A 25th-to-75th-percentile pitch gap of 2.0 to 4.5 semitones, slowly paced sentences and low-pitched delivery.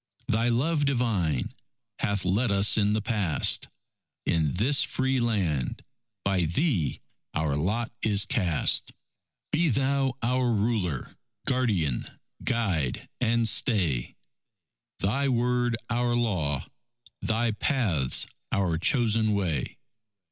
No: wide, 5.5 semitones; slow, 105 wpm; low, 110 Hz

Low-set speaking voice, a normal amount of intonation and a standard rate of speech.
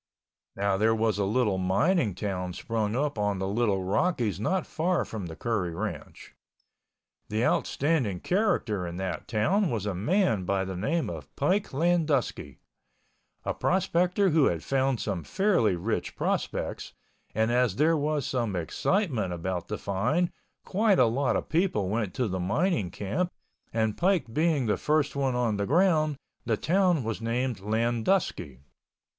No: low, 115 Hz; wide, 8.1 semitones; average, 160 wpm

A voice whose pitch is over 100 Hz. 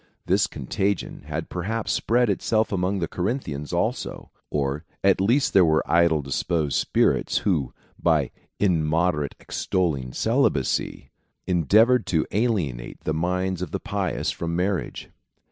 No: very low, 90 Hz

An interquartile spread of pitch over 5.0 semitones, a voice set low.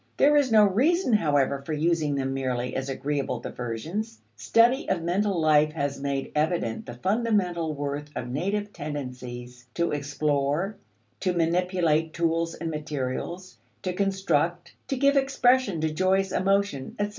No: wide, 5.6 semitones; medium, 165 Hz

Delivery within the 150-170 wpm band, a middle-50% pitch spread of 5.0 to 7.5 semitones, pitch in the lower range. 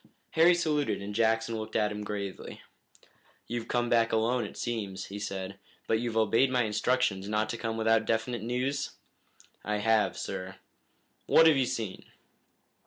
No: average, 160 wpm; narrow, 2.6 semitones; low, 115 Hz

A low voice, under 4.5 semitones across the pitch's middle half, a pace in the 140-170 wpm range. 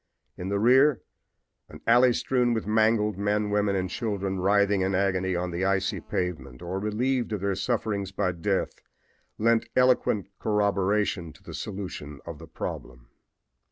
Yes: low, 100 Hz; average, 2.8 semitones; average, 155 wpm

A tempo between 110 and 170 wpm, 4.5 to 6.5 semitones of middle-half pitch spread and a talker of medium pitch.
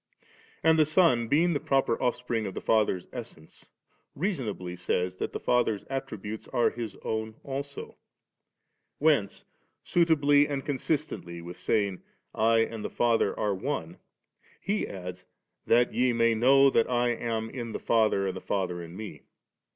No: average, 155 wpm; average, 5.1 semitones; low, 115 Hz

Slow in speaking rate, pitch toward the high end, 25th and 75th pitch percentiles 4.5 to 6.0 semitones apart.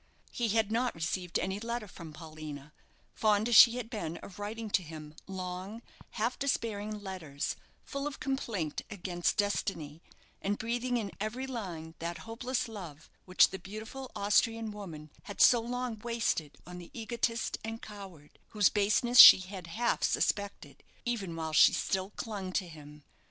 No: average, 155 wpm; high, 205 Hz; average, 4.9 semitones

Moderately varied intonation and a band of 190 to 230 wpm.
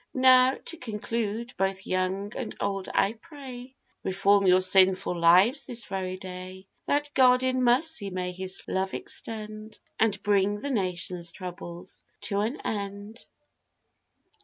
No: average, 4.5 semitones; slow, 135 wpm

